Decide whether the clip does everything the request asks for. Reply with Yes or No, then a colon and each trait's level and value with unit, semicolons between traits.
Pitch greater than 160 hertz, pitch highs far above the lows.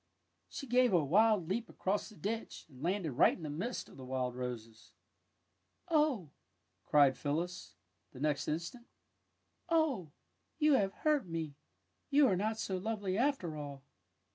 Yes: medium, 185 Hz; wide, 7.9 semitones